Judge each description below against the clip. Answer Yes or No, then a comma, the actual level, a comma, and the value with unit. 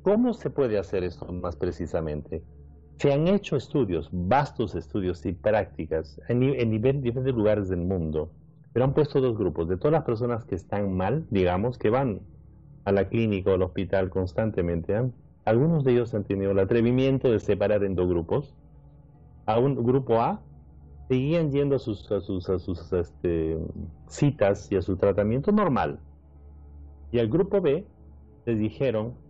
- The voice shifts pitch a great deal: Yes, wide, 7.0 semitones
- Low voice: Yes, low, 100 Hz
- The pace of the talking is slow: No, average, 170 wpm